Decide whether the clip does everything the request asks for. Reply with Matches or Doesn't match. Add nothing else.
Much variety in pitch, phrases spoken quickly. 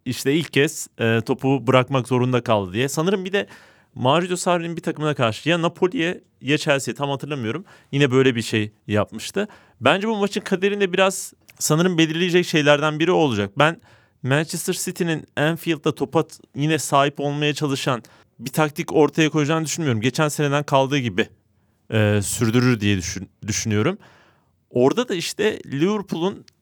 Matches